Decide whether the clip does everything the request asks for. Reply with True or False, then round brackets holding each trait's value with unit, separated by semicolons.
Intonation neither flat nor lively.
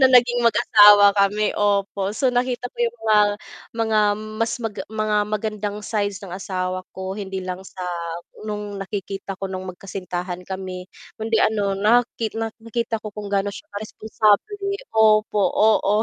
False (2.2 semitones)